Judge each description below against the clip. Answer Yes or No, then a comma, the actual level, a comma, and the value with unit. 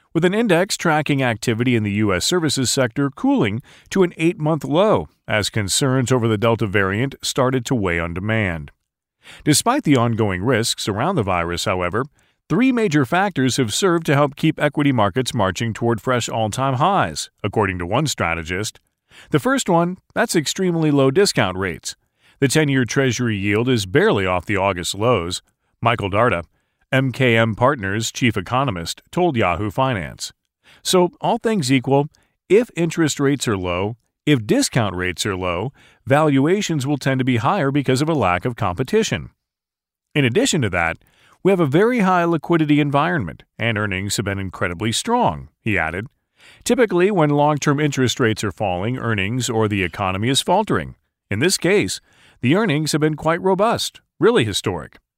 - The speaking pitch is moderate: No, low, 130 Hz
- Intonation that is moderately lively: No, wide, 6.5 semitones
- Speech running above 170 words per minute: No, average, 165 wpm